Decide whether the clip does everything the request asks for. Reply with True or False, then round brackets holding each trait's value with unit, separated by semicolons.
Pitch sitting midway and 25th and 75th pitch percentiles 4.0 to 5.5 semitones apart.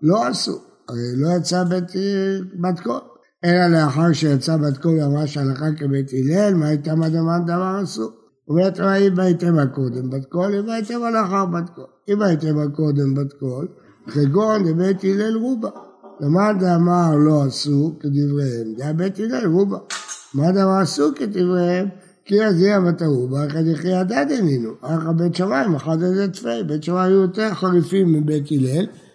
True (170 Hz; 4.5 semitones)